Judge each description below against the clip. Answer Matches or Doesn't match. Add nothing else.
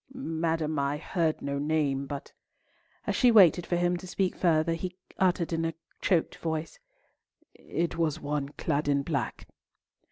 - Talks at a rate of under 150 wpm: Matches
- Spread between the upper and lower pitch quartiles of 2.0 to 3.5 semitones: Matches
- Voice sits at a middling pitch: Matches